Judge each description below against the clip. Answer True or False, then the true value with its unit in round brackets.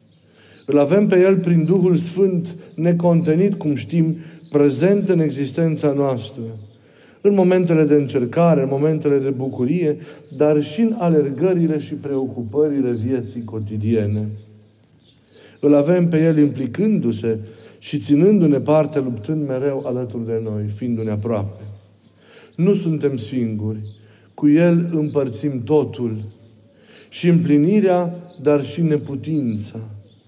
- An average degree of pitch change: False (6.2 semitones)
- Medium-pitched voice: True (145 Hz)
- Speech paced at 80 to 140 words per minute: True (115 wpm)